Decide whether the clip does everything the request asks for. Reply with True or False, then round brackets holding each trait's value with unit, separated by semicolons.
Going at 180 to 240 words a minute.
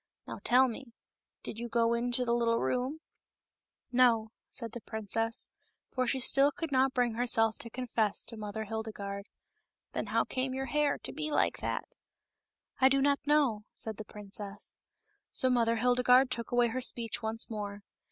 True (185 wpm)